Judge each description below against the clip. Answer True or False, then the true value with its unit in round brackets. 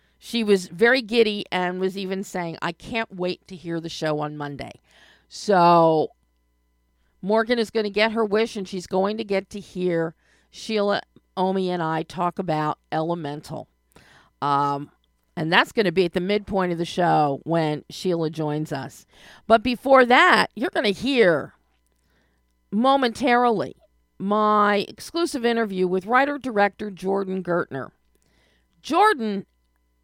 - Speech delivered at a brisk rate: False (145 wpm)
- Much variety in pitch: True (5.8 semitones)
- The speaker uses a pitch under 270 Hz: True (185 Hz)